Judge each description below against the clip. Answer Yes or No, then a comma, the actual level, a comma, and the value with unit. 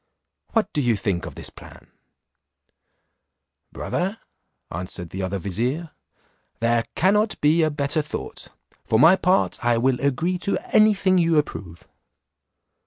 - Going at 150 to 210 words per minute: No, slow, 135 wpm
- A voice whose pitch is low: No, medium, 145 Hz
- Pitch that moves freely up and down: Yes, wide, 8.2 semitones